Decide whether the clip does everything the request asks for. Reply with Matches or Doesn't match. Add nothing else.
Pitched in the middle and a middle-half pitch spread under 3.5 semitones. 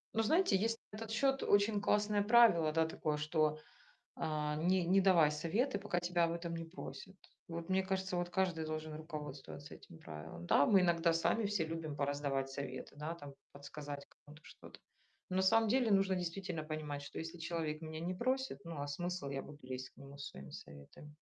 Doesn't match